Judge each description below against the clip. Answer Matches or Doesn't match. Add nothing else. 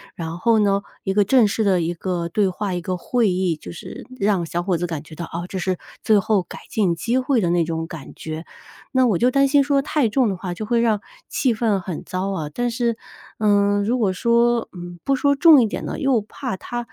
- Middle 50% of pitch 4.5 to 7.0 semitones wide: Matches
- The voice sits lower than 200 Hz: Doesn't match